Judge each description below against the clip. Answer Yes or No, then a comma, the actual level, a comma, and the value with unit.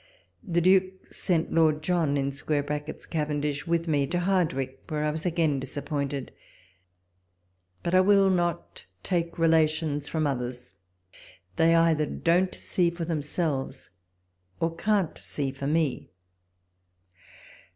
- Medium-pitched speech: Yes, medium, 160 Hz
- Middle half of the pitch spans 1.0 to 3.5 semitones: Yes, average, 3.1 semitones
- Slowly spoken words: Yes, slow, 115 wpm